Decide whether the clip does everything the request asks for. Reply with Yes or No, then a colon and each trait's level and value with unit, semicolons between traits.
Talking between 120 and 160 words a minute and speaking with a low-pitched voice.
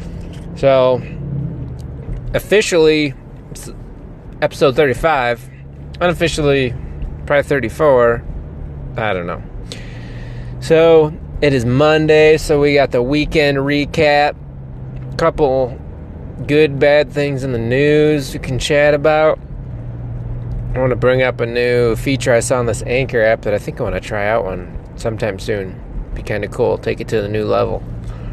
Yes: slow, 135 wpm; low, 130 Hz